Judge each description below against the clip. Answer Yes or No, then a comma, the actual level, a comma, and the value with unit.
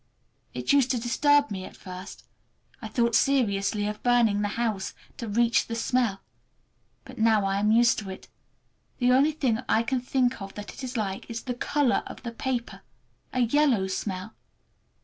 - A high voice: Yes, high, 230 Hz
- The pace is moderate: Yes, average, 175 wpm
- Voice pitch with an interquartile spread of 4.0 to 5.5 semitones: No, average, 3.5 semitones